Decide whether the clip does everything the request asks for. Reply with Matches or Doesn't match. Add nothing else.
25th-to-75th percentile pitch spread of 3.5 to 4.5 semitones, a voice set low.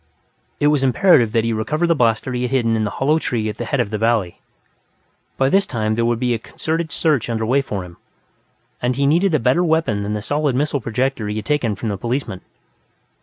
Doesn't match